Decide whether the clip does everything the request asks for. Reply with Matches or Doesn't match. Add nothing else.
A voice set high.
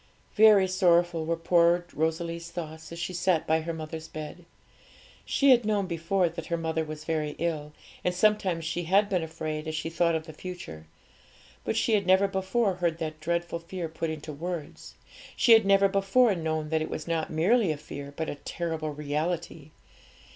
Doesn't match